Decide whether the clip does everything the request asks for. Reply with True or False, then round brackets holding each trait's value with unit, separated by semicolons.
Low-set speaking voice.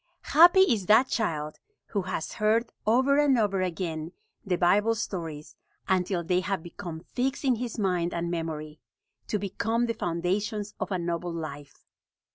False (190 Hz)